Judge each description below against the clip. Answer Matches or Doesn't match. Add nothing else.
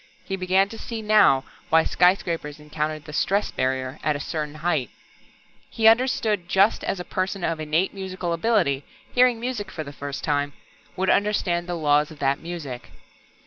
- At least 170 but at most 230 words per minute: Matches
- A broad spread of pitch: Doesn't match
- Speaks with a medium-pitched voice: Matches